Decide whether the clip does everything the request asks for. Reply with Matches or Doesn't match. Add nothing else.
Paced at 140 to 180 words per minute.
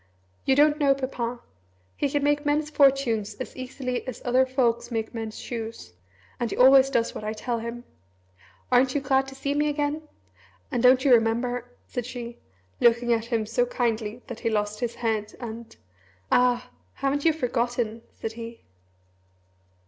Matches